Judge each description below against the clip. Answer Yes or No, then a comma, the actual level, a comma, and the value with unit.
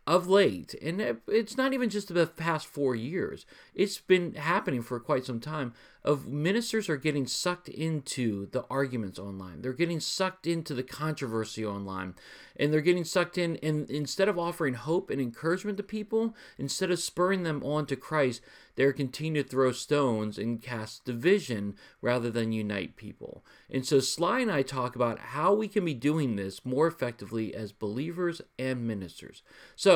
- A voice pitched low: No, medium, 145 Hz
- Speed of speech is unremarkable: Yes, average, 175 wpm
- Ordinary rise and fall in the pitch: No, wide, 6.1 semitones